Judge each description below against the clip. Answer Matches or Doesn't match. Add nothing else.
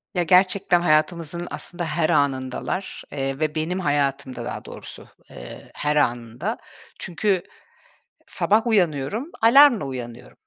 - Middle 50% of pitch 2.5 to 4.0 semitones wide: Doesn't match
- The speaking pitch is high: Doesn't match